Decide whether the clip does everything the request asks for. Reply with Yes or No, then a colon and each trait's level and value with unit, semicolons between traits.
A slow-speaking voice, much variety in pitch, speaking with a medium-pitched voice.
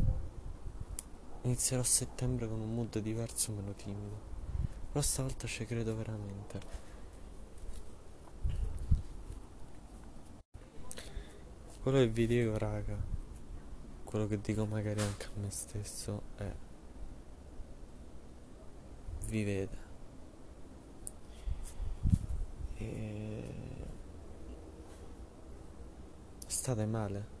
No: slow, 70 wpm; wide, 6.1 semitones; very low, 90 Hz